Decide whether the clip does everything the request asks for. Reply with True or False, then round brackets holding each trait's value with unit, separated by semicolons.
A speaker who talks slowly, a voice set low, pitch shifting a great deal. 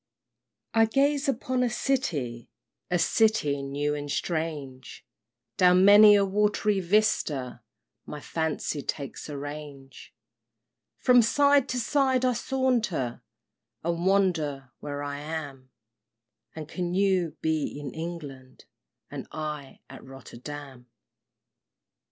False (110 wpm; 160 Hz; 6.8 semitones)